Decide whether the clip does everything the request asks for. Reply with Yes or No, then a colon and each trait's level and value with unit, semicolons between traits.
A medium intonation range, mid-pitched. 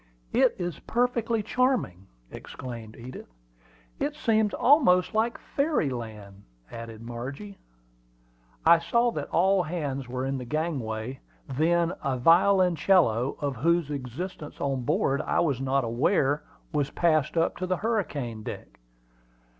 No: wide, 6.7 semitones; medium, 150 Hz